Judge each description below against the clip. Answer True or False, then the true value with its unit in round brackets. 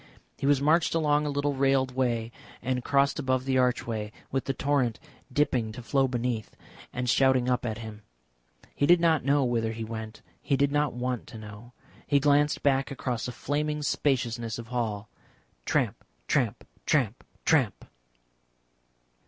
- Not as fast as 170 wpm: True (160 wpm)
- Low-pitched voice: True (130 Hz)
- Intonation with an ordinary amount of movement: True (3.3 semitones)